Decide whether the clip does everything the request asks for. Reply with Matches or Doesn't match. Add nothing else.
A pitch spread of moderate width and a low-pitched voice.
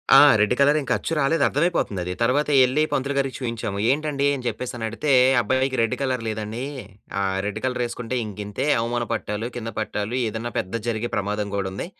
Matches